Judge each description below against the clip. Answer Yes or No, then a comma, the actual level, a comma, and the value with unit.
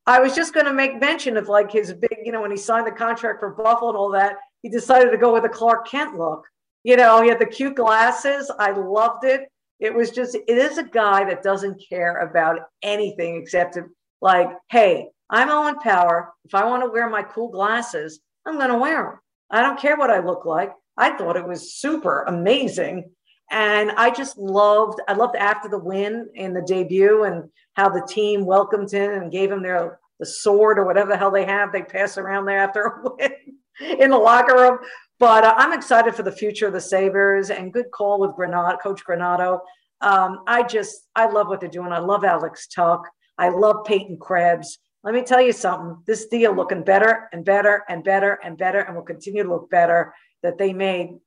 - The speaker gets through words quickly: Yes, fast, 215 wpm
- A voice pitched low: No, high, 205 Hz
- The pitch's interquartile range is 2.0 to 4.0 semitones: Yes, average, 3.7 semitones